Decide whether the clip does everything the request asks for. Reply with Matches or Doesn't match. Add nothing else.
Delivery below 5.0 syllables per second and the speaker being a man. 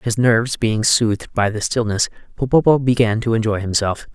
Doesn't match